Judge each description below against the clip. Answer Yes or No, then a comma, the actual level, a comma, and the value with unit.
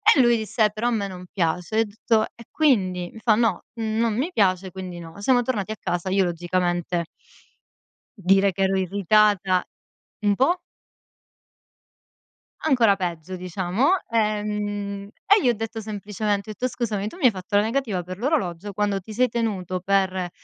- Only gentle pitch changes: No, average, 3.3 semitones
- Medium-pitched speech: No, high, 205 Hz